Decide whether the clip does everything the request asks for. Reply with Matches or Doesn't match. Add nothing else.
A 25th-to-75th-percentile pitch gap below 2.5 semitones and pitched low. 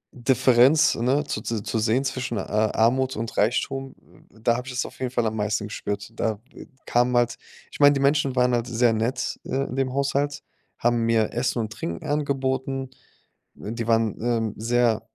Doesn't match